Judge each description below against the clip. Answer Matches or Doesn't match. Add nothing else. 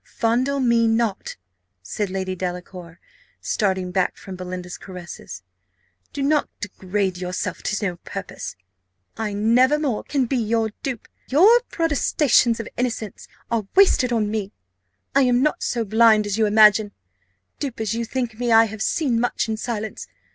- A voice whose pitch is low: Doesn't match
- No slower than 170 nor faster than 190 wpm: Doesn't match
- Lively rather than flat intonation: Doesn't match